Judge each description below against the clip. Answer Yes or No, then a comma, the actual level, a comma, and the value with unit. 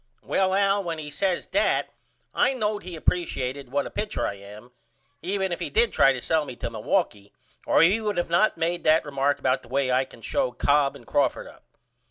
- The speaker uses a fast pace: Yes, fast, 215 wpm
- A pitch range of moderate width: No, wide, 6.5 semitones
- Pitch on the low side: No, medium, 155 Hz